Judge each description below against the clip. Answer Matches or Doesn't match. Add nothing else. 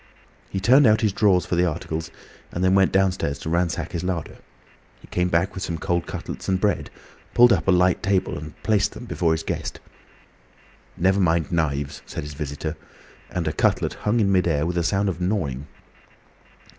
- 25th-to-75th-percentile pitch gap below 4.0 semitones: Matches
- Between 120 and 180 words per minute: Doesn't match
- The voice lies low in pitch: Matches